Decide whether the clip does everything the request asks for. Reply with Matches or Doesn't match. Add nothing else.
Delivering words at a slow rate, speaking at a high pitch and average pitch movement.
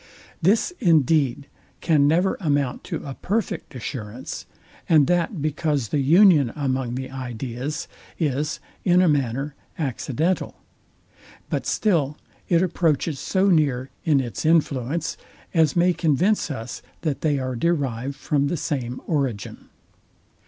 Doesn't match